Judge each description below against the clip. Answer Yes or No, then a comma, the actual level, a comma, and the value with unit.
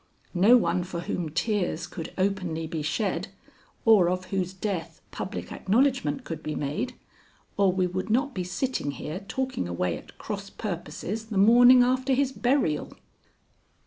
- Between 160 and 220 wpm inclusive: No, average, 150 wpm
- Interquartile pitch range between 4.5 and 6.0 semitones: Yes, wide, 5.6 semitones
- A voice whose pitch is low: No, high, 190 Hz